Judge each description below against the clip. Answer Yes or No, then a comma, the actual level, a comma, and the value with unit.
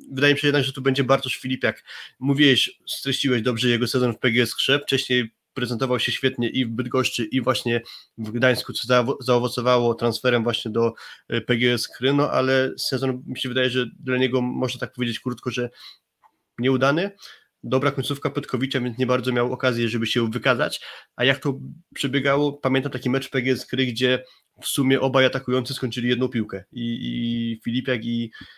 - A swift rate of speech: Yes, fast, 170 wpm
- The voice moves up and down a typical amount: No, narrow, 1.6 semitones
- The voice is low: Yes, low, 130 Hz